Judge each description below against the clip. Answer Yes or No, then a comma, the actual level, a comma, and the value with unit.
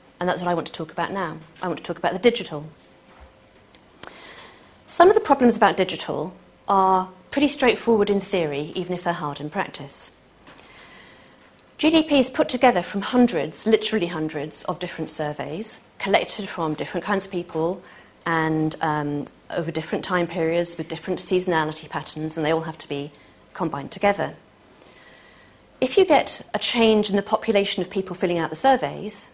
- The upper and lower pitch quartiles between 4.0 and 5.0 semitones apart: Yes, average, 4.6 semitones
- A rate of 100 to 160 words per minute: No, average, 170 wpm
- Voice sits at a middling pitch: Yes, medium, 180 Hz